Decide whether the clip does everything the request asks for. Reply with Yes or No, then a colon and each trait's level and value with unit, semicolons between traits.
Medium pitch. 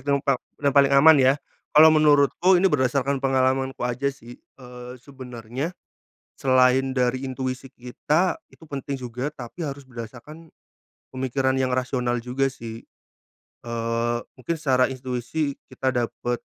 No: low, 130 Hz